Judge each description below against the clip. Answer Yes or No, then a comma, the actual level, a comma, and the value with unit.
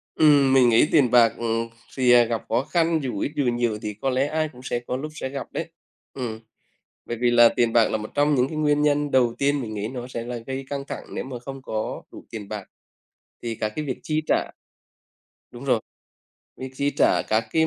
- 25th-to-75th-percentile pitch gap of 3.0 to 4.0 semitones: Yes, average, 3.4 semitones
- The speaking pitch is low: Yes, low, 125 Hz